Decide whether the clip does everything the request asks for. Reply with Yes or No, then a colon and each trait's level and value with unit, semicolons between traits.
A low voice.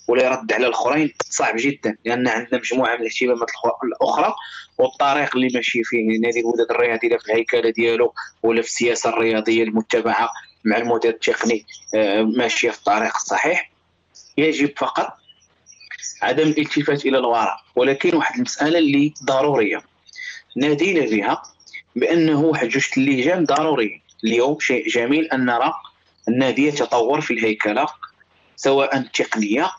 Yes: low, 120 Hz